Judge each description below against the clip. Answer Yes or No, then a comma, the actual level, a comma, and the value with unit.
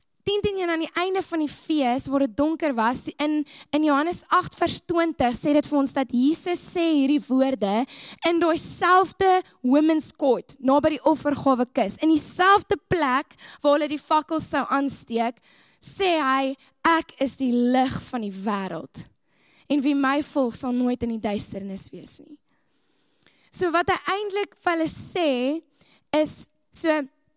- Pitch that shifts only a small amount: No, average, 3.7 semitones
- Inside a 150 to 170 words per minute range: Yes, average, 160 wpm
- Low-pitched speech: No, very high, 295 Hz